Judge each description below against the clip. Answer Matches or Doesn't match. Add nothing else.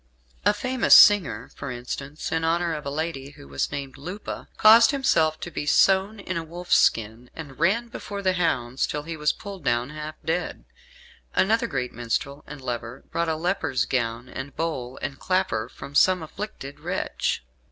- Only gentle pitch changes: Doesn't match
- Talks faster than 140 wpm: Matches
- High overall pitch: Doesn't match